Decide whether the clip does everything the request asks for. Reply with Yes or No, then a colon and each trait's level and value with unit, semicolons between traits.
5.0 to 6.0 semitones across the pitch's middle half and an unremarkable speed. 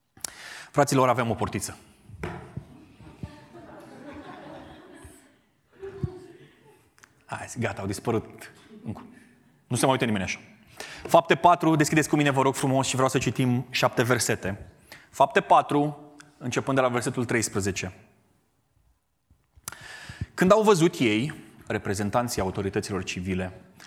No: wide, 5.4 semitones; slow, 105 wpm